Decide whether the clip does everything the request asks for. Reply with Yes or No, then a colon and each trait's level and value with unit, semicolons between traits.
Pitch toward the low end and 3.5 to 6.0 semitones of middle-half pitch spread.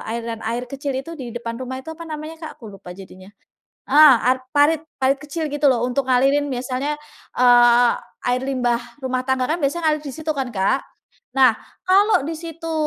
No: very high, 265 Hz; average, 3.8 semitones